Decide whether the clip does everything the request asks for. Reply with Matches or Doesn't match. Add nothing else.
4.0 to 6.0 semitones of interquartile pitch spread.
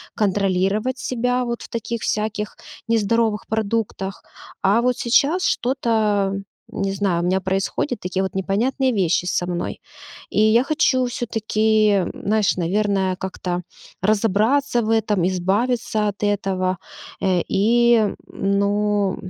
Doesn't match